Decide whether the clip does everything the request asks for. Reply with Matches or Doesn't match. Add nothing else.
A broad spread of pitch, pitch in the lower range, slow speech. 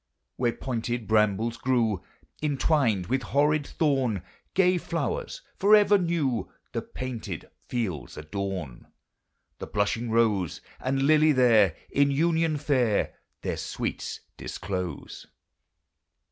Matches